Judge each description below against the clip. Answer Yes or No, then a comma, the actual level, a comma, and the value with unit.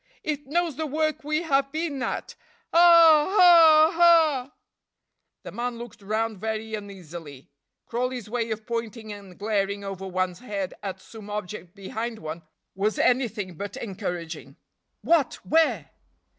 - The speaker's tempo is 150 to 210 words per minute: No, slow, 135 wpm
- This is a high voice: Yes, high, 225 Hz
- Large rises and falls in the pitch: Yes, wide, 7.0 semitones